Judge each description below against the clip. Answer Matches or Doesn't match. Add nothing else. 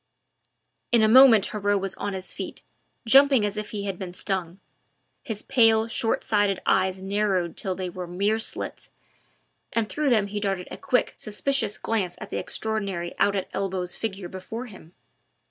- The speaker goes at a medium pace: Matches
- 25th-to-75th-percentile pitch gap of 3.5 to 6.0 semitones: Doesn't match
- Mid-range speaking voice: Doesn't match